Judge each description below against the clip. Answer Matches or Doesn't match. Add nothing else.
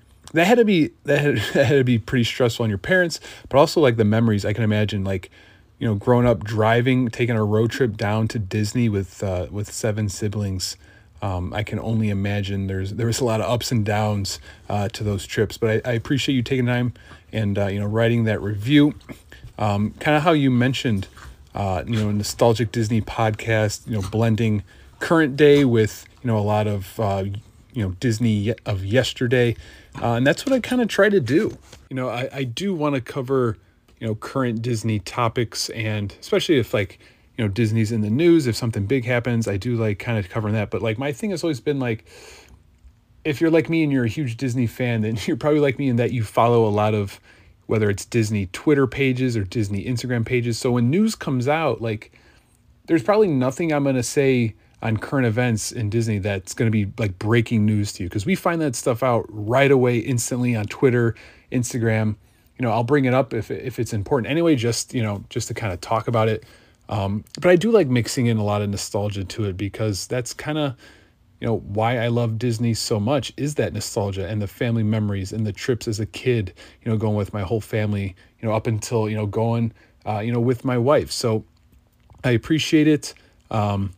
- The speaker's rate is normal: Doesn't match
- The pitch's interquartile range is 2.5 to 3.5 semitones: Matches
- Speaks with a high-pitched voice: Doesn't match